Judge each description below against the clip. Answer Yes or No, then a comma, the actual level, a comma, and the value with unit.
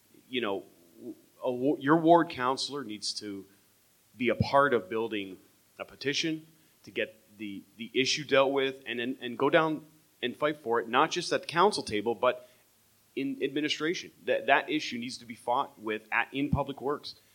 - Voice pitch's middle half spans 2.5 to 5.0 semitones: No, wide, 5.4 semitones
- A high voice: No, low, 135 Hz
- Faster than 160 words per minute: Yes, average, 180 wpm